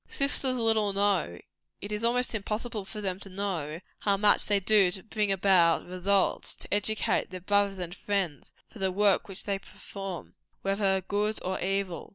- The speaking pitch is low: No, high, 200 Hz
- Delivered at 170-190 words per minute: Yes, average, 180 wpm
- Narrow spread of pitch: Yes, narrow, 1.9 semitones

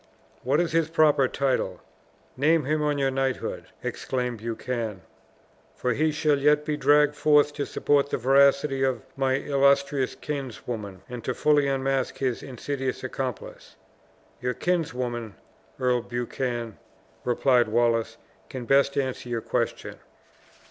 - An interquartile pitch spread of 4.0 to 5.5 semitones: No, average, 2.9 semitones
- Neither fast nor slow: No, slow, 130 wpm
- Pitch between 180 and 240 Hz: No, low, 135 Hz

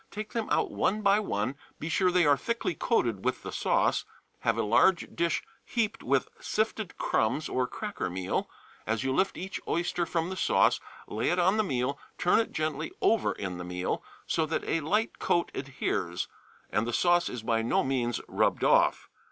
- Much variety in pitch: Yes, wide, 8.4 semitones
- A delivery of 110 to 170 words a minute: No, average, 190 wpm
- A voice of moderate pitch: Yes, medium, 160 Hz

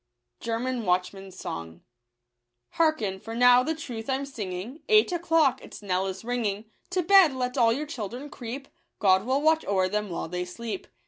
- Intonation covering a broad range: Yes, wide, 6.5 semitones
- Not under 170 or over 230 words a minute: No, average, 160 wpm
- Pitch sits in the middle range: No, high, 235 Hz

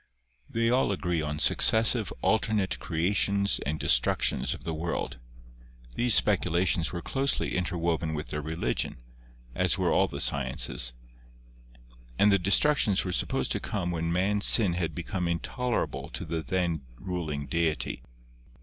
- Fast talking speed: No, average, 140 wpm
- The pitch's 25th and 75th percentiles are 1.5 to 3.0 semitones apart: No, average, 3.9 semitones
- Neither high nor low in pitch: No, very low, 90 Hz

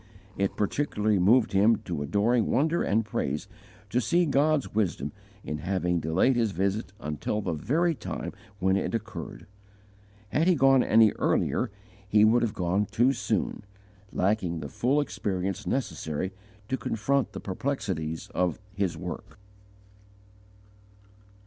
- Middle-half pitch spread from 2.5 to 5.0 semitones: No, wide, 5.6 semitones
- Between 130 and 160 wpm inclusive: Yes, slow, 135 wpm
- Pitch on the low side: Yes, low, 105 Hz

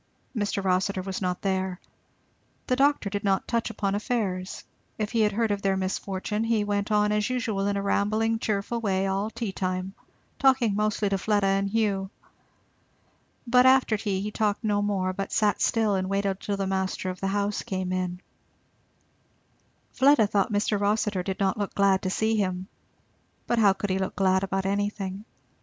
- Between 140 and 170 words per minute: No, average, 180 wpm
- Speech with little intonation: Yes, narrow, 1.9 semitones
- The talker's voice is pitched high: Yes, high, 200 Hz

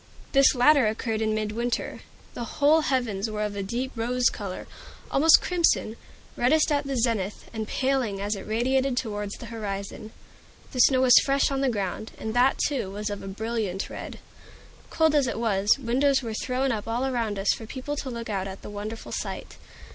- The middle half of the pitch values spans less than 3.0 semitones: No, average, 3.9 semitones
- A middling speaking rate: Yes, average, 190 wpm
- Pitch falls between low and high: No, high, 230 Hz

